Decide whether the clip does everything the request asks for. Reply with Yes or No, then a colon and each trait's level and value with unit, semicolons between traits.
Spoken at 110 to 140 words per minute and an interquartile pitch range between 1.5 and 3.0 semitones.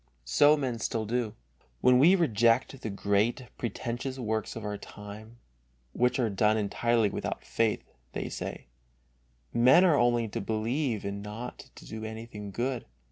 No: average, 150 wpm; average, 2.7 semitones